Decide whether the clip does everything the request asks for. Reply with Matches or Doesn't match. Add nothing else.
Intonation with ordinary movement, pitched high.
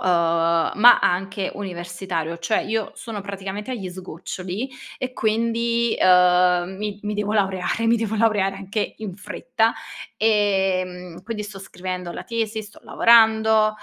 Matches